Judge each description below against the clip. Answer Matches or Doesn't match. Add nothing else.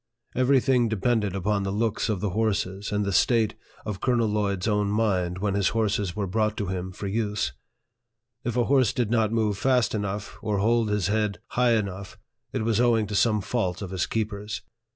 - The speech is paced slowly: Doesn't match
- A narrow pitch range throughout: Matches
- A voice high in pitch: Doesn't match